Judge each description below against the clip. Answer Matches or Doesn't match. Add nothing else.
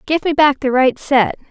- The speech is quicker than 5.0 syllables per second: Doesn't match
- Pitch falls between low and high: Doesn't match